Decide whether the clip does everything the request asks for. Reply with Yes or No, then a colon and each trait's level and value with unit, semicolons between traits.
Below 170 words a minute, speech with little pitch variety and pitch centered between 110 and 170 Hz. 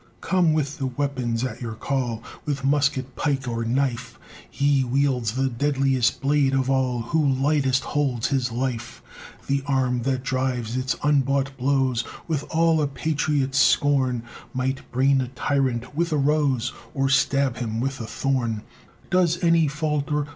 Yes: average, 155 wpm; narrow, 2.3 semitones; low, 135 Hz